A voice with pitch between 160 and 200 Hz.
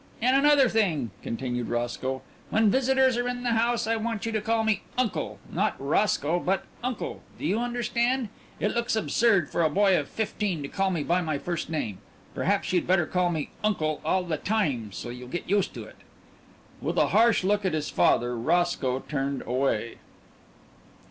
Yes: high, 190 Hz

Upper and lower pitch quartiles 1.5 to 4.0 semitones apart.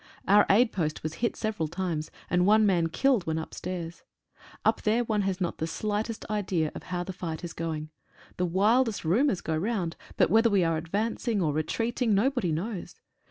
No: average, 4.8 semitones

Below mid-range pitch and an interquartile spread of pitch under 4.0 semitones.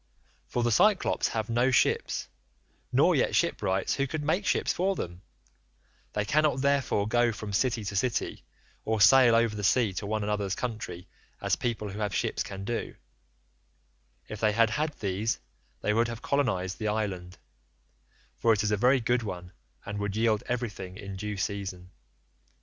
Yes: low, 110 Hz; average, 3.4 semitones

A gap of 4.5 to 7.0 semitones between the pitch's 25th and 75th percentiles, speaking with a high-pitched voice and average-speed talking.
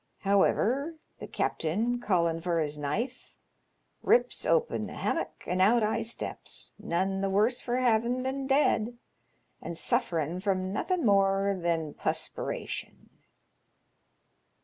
No: average, 5.2 semitones; high, 205 Hz; slow, 120 wpm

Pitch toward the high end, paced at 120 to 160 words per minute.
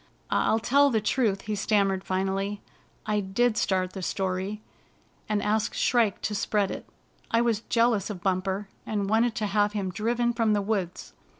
No: high, 210 Hz; average, 180 wpm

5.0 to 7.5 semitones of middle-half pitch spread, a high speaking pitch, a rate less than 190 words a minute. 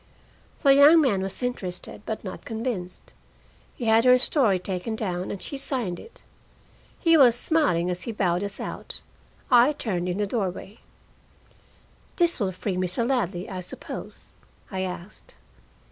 Yes: wide, 5.5 semitones; high, 210 Hz; average, 150 wpm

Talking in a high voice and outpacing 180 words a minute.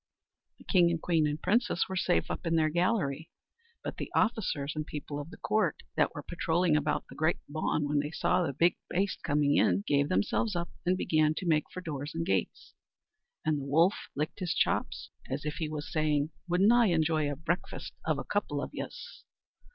No: medium, 155 Hz; fast, 205 wpm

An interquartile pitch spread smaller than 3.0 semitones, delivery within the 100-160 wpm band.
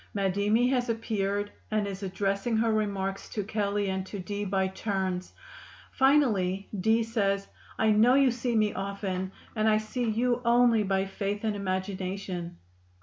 Yes: narrow, 2.5 semitones; average, 150 wpm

